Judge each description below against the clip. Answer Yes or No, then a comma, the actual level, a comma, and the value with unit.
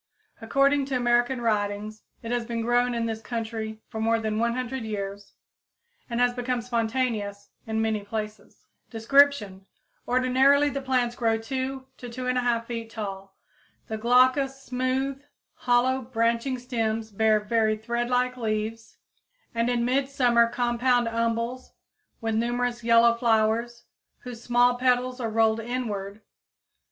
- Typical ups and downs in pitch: No, narrow, 2.2 semitones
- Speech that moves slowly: Yes, slow, 130 wpm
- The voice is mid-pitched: No, high, 235 Hz